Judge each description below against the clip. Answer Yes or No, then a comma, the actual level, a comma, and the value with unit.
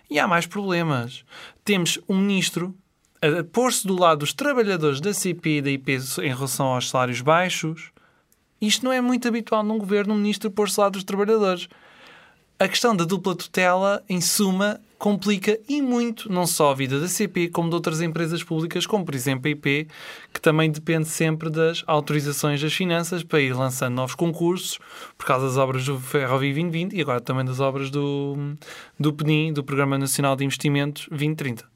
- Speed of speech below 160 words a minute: No, fast, 185 wpm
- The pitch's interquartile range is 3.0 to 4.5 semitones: No, wide, 5.4 semitones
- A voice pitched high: No, medium, 165 Hz